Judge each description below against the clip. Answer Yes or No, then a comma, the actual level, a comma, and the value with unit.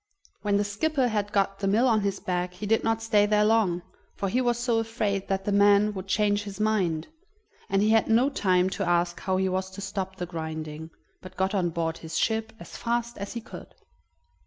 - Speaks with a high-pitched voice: Yes, high, 200 Hz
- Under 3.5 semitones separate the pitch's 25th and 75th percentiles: Yes, average, 3.0 semitones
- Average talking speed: No, fast, 220 wpm